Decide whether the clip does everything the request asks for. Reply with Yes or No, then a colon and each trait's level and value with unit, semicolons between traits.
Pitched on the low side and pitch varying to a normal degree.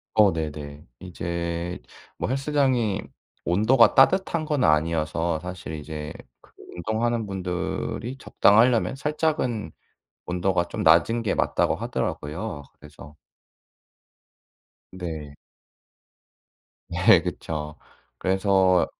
No: very low, 90 Hz; wide, 6.2 semitones